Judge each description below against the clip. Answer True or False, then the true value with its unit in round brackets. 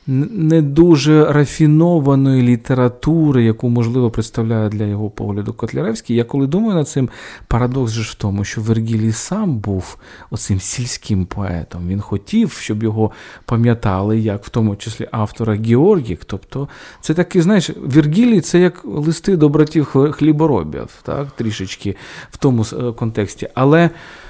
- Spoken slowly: False (135 wpm)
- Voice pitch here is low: True (120 Hz)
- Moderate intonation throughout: False (5.9 semitones)